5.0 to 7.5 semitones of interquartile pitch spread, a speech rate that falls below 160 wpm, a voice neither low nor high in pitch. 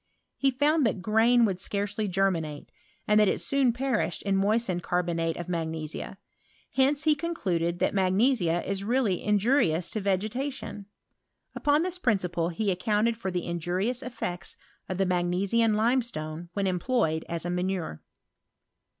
No: average, 5.3 semitones; average, 140 wpm; high, 195 Hz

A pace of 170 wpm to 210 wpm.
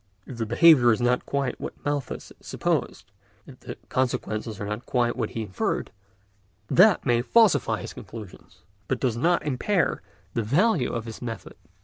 No: average, 160 wpm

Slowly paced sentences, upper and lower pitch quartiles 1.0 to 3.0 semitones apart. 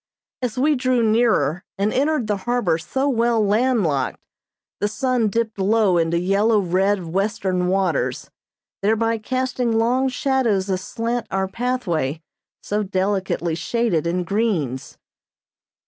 No: slow, 125 wpm; average, 4.3 semitones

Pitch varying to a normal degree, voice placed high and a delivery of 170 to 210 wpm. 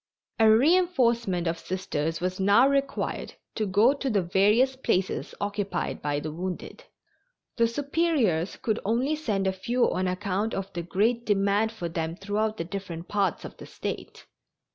No: average, 4.2 semitones; high, 200 Hz; average, 160 wpm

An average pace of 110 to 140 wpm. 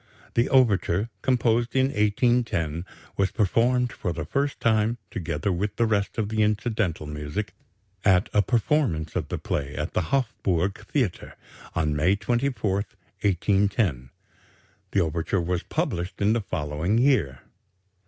Yes: slow, 135 wpm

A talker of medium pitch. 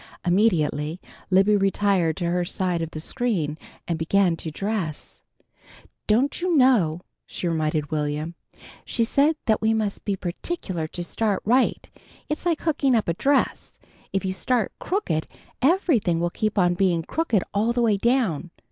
No: high, 195 Hz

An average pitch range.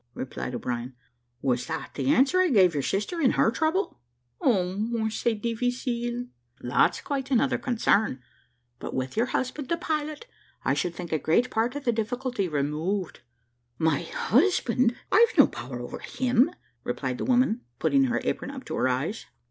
No: wide, 7.9 semitones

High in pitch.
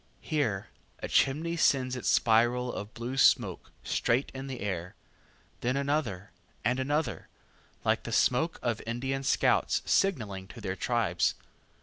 No: low, 125 Hz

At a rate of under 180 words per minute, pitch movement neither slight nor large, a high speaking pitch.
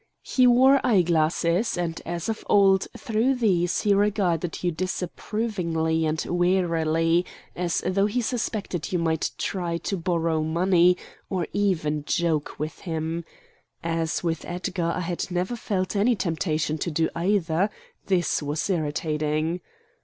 No: average, 140 wpm; average, 3.2 semitones; medium, 175 Hz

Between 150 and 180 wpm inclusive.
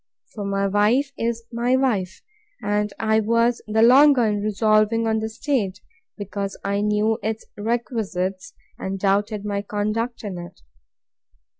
No: average, 140 wpm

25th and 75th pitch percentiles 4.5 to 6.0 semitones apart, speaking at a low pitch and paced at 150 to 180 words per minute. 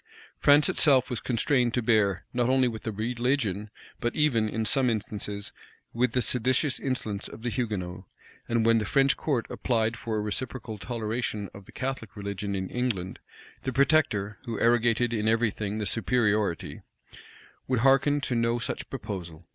No: average, 3.2 semitones; low, 115 Hz; average, 165 wpm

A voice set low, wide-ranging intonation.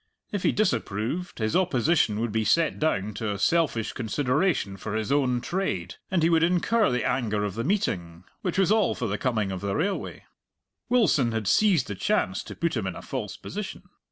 Yes: low, 125 Hz; wide, 8.5 semitones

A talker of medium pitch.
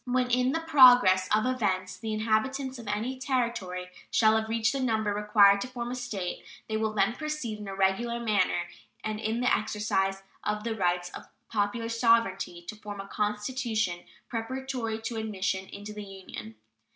No: high, 220 Hz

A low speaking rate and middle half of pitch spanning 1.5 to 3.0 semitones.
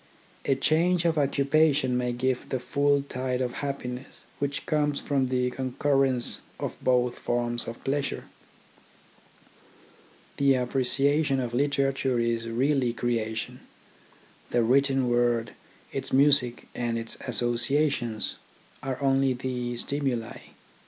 Yes: slow, 115 wpm; narrow, 2.5 semitones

